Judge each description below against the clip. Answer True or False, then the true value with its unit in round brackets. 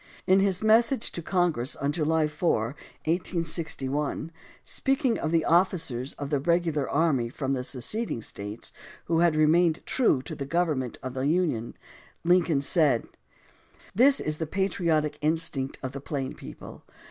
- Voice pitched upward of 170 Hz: False (155 Hz)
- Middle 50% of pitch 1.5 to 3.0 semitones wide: False (4.2 semitones)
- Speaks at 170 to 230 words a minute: False (145 wpm)